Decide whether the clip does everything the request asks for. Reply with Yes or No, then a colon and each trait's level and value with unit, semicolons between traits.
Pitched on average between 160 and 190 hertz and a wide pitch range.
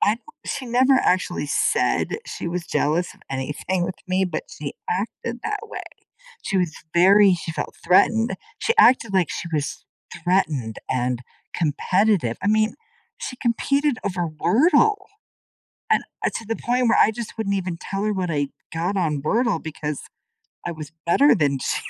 Yes: medium, 185 Hz; wide, 6.4 semitones